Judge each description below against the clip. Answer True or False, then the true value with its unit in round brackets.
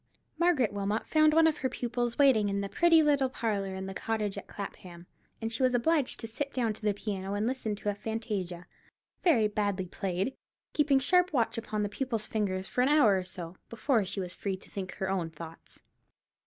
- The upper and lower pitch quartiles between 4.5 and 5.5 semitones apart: True (5.0 semitones)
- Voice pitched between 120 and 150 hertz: False (215 Hz)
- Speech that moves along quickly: True (210 wpm)